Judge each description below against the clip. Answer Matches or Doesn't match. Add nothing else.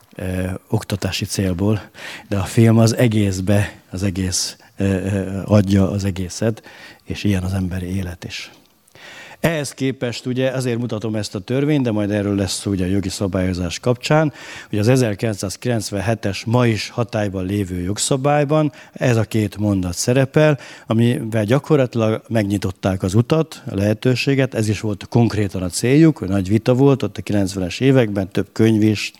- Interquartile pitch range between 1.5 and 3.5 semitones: Doesn't match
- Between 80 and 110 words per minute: Doesn't match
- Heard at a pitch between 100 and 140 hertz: Matches